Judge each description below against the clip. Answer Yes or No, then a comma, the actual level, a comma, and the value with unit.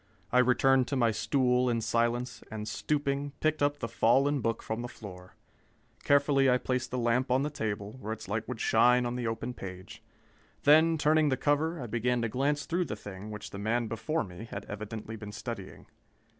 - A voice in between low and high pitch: No, low, 120 Hz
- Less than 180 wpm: No, average, 200 wpm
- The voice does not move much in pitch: No, average, 3.9 semitones